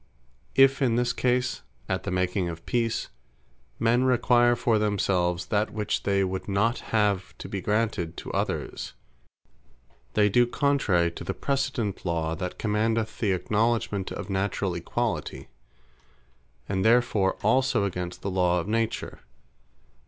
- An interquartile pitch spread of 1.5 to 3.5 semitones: No, average, 4.1 semitones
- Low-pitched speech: Yes, low, 105 Hz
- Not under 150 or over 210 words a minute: No, slow, 135 wpm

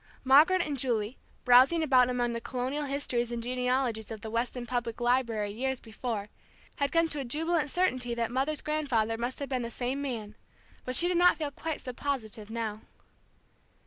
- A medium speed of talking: Yes, average, 180 wpm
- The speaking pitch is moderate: No, very high, 250 Hz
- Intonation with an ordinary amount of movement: Yes, average, 3.3 semitones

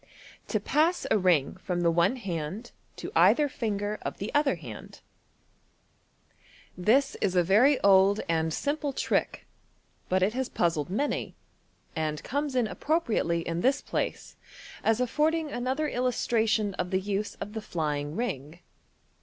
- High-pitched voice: Yes, high, 205 Hz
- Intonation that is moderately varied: No, wide, 6.9 semitones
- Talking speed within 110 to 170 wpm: Yes, average, 150 wpm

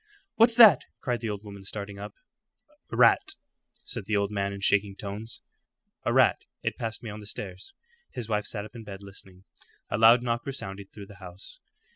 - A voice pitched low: Yes, low, 105 Hz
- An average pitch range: No, narrow, 2.3 semitones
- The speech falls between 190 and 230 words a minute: Yes, average, 195 wpm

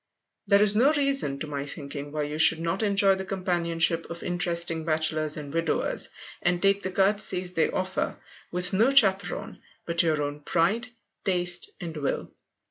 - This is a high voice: No, medium, 175 Hz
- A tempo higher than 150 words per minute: Yes, average, 165 wpm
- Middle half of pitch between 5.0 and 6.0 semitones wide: No, average, 3.7 semitones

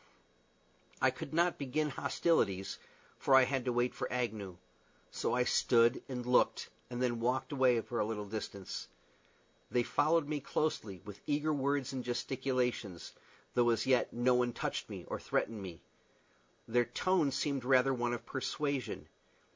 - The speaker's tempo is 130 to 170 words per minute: Yes, average, 155 wpm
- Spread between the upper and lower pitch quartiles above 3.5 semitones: No, narrow, 2.6 semitones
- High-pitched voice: No, low, 125 Hz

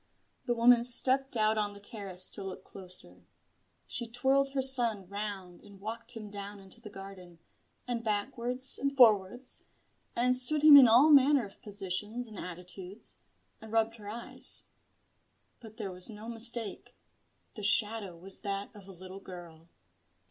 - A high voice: Yes, high, 215 Hz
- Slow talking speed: No, average, 155 wpm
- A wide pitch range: No, average, 3.8 semitones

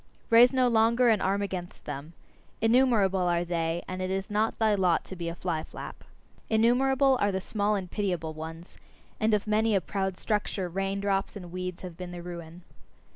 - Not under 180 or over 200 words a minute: Yes, average, 190 wpm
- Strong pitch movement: No, average, 3.7 semitones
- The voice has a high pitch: Yes, high, 195 Hz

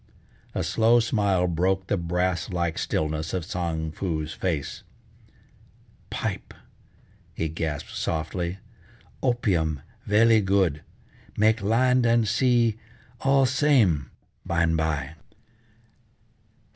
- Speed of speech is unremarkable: No, slow, 100 wpm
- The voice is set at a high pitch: No, very low, 90 Hz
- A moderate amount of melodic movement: No, wide, 5.8 semitones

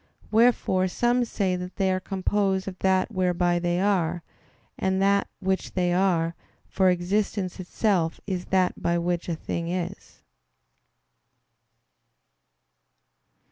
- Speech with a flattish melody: Yes, narrow, 1.8 semitones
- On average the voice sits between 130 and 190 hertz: Yes, medium, 185 Hz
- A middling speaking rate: No, slow, 120 wpm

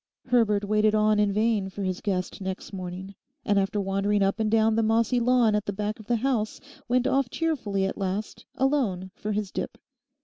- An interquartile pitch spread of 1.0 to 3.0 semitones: Yes, narrow, 2.6 semitones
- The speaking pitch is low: No, high, 210 Hz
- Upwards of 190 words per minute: Yes, average, 200 wpm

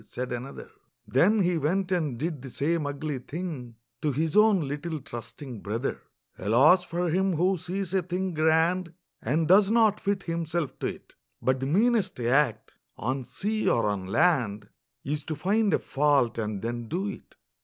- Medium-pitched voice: Yes, medium, 155 Hz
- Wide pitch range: Yes, wide, 6.2 semitones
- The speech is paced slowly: No, average, 170 wpm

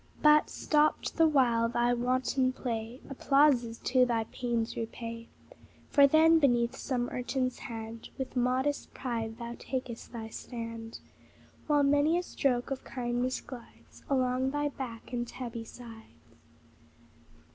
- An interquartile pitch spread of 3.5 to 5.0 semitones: No, average, 2.7 semitones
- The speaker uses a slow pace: Yes, slow, 130 wpm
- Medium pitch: No, very high, 250 Hz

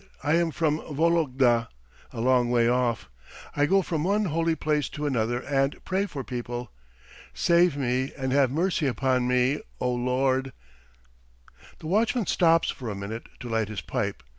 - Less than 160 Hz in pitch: Yes, low, 135 Hz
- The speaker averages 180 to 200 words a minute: No, average, 165 wpm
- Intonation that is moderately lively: Yes, average, 4.8 semitones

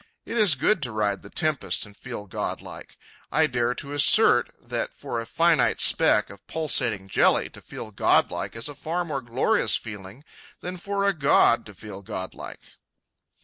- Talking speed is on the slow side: No, average, 170 wpm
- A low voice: Yes, low, 125 Hz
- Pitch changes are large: Yes, wide, 7.2 semitones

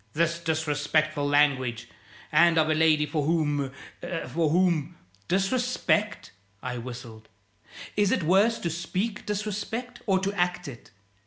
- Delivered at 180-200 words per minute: No, slow, 135 wpm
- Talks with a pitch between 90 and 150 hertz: No, medium, 160 Hz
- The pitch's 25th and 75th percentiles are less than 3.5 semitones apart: No, average, 4.6 semitones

